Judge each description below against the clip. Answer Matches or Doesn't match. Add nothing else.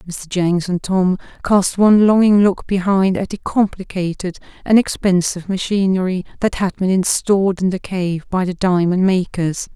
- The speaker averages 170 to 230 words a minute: Doesn't match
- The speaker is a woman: Matches